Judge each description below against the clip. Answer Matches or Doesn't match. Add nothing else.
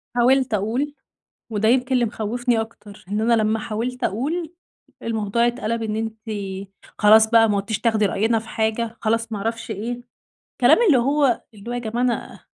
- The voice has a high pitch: Matches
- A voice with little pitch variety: Matches